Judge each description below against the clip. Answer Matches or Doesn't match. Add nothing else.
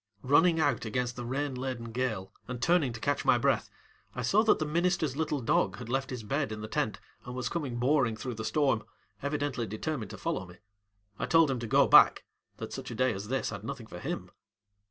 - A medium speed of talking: Doesn't match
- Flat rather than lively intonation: Doesn't match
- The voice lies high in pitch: Doesn't match